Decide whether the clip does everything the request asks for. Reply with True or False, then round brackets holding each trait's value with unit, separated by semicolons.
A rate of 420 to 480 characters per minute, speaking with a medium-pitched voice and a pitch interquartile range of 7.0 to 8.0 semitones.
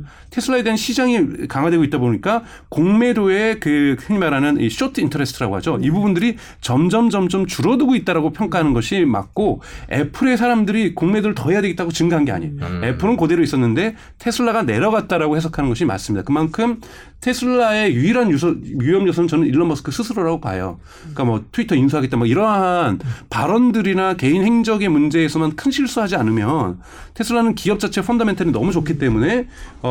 True (430 characters per minute; 175 Hz; 7.4 semitones)